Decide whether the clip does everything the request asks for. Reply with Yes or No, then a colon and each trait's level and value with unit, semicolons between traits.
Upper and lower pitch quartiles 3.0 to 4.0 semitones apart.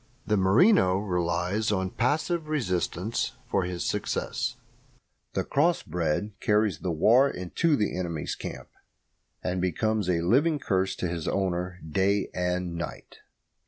Yes: average, 3.7 semitones